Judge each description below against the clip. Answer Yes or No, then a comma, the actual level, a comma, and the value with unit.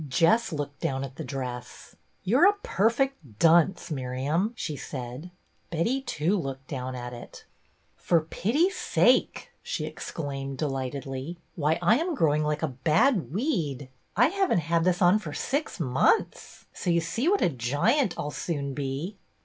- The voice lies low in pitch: No, medium, 160 Hz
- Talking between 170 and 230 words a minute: Yes, average, 175 wpm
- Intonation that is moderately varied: No, wide, 7.3 semitones